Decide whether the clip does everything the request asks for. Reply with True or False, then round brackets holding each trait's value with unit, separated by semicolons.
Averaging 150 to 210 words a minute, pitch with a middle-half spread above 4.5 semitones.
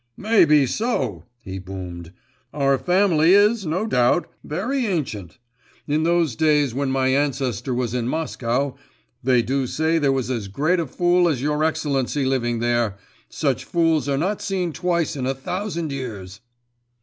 True (160 wpm; 5.4 semitones)